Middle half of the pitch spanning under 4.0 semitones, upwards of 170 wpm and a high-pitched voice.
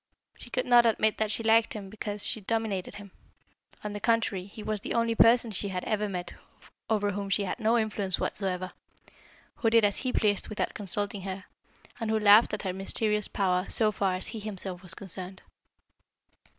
Yes: narrow, 2.4 semitones; average, 190 wpm; high, 205 Hz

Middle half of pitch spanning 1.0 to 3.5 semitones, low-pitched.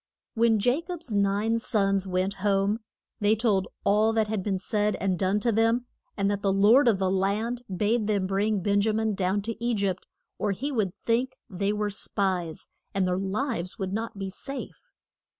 No: narrow, 2.5 semitones; high, 205 Hz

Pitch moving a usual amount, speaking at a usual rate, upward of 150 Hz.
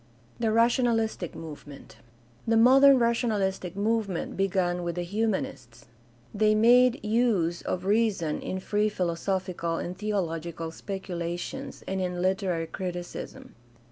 No: average, 4.4 semitones; slow, 115 wpm; high, 190 Hz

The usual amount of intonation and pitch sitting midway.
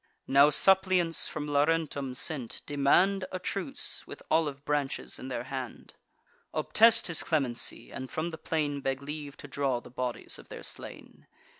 Yes: average, 3.4 semitones; medium, 145 Hz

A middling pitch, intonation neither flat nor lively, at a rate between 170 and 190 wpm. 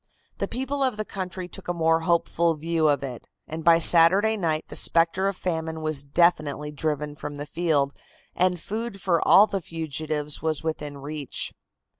Yes: medium, 165 Hz; average, 3.2 semitones; average, 175 wpm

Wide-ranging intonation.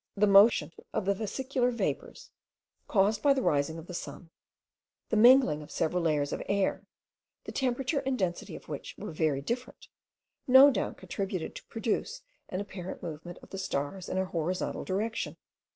Yes: wide, 6.0 semitones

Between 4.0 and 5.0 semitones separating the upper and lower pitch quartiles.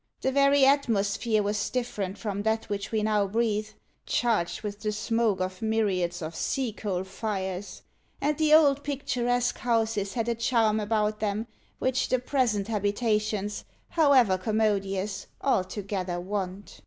No: average, 3.0 semitones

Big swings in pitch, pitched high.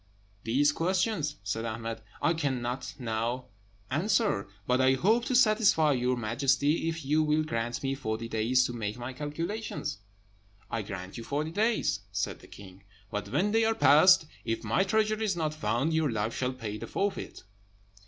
No: wide, 6.3 semitones; low, 135 Hz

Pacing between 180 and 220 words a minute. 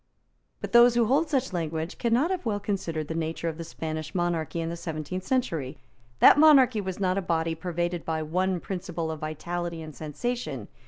Yes: average, 190 wpm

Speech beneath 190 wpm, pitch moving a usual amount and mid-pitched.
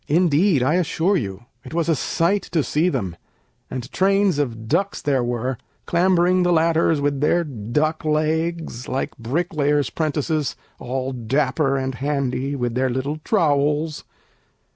Yes: average, 140 wpm; average, 4.2 semitones; medium, 150 Hz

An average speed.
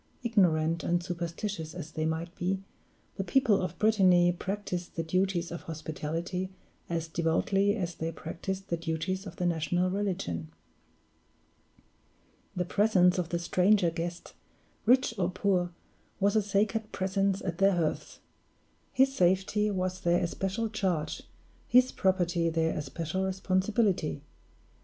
No: slow, 130 wpm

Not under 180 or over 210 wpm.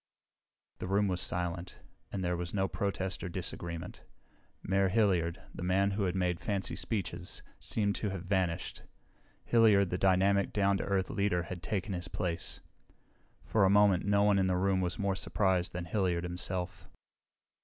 No: average, 165 wpm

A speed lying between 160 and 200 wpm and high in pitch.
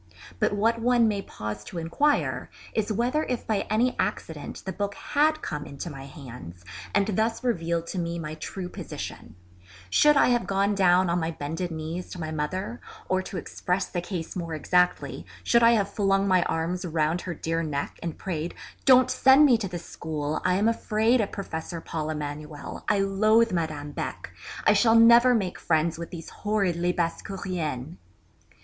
No: average, 180 wpm; medium, 180 Hz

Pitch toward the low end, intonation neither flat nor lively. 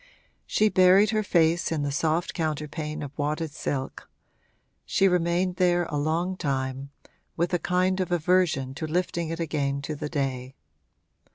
No: medium, 160 Hz; average, 3.7 semitones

